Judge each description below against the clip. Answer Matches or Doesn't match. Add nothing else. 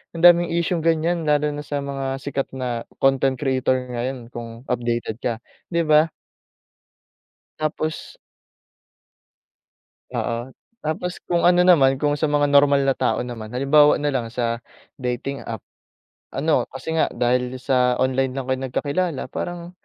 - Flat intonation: Doesn't match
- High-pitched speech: Doesn't match